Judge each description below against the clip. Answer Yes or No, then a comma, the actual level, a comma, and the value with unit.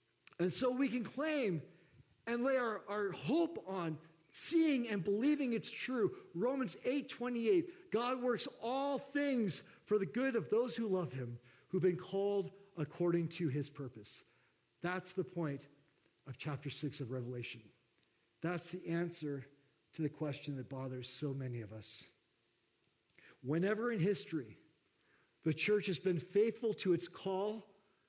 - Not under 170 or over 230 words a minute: No, average, 145 wpm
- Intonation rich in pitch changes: Yes, wide, 7.8 semitones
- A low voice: No, medium, 185 Hz